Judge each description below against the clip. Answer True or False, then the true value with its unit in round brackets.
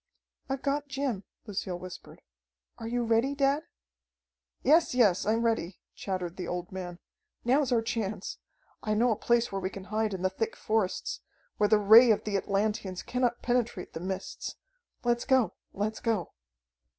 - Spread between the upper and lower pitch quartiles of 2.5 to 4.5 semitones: True (4.0 semitones)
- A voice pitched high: True (220 Hz)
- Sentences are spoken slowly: False (165 wpm)